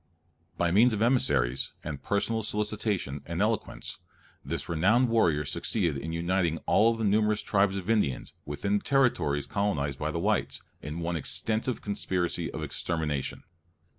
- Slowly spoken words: No, average, 145 wpm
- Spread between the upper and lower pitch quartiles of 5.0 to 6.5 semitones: Yes, wide, 5.4 semitones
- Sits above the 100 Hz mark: No, very low, 95 Hz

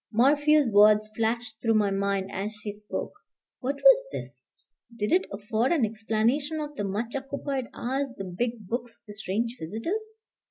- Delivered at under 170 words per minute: Yes, average, 160 wpm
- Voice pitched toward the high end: Yes, high, 230 Hz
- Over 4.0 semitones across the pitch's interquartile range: Yes, average, 4.8 semitones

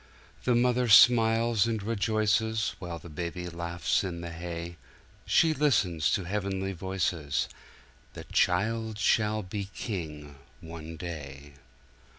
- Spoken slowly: Yes, slow, 115 wpm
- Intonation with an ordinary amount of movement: Yes, average, 4.8 semitones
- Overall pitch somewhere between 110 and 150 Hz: No, very low, 95 Hz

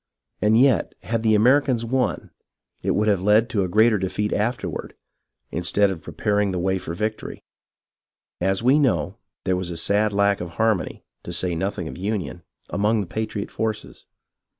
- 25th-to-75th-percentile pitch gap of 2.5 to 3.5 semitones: Yes, average, 2.9 semitones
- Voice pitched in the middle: No, low, 105 Hz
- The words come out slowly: No, average, 170 wpm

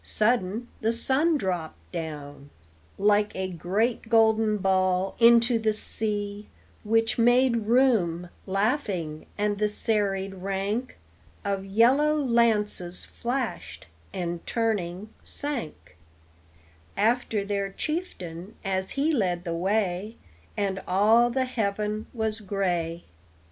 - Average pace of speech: No, slow, 105 wpm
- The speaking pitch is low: No, high, 210 Hz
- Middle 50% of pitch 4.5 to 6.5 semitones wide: No, average, 3.6 semitones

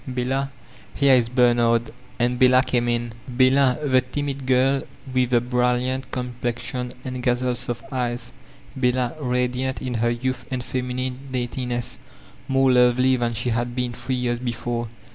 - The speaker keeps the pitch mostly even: Yes, narrow, 1.2 semitones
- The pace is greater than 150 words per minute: No, average, 145 wpm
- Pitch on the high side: No, low, 125 Hz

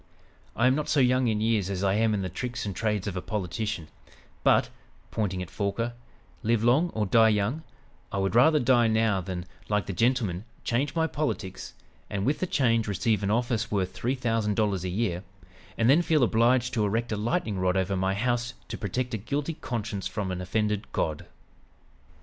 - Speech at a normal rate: Yes, average, 195 wpm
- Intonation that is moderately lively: Yes, average, 3.7 semitones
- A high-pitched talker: No, low, 110 Hz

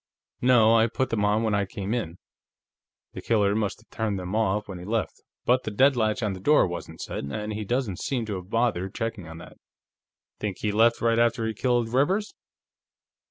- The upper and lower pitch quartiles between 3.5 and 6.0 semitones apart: No, average, 2.7 semitones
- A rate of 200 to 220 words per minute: Yes, fast, 205 wpm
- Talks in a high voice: No, low, 110 Hz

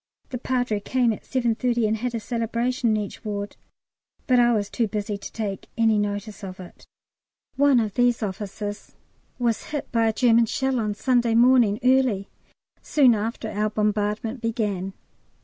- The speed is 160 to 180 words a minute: Yes, average, 165 wpm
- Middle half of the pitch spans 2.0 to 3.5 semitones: Yes, average, 2.8 semitones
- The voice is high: Yes, high, 225 Hz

